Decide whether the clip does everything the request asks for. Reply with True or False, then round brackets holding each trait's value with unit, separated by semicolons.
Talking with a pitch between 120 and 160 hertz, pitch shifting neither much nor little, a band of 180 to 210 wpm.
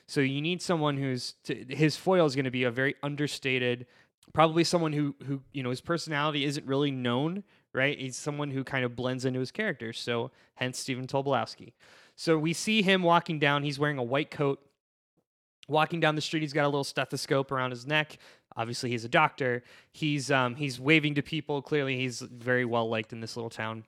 True (140 Hz; 3.2 semitones; 205 wpm)